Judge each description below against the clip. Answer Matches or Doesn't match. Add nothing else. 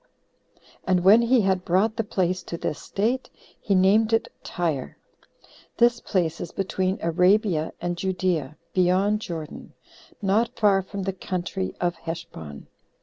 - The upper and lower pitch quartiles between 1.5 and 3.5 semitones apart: Matches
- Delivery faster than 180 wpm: Doesn't match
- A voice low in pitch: Doesn't match